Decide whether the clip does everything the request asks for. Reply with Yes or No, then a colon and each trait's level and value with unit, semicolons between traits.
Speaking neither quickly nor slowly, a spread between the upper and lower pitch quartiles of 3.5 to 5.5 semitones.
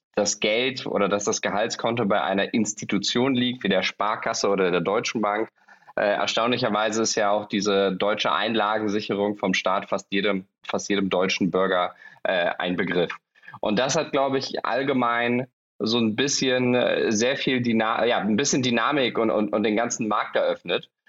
Yes: average, 160 wpm; average, 3.8 semitones